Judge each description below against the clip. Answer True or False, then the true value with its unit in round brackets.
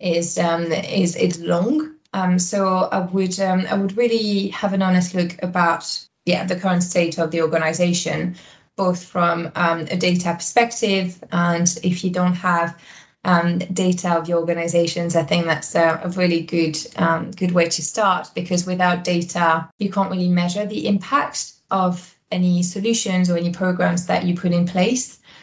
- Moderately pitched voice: True (180 Hz)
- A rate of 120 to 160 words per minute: False (170 wpm)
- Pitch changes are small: True (1.8 semitones)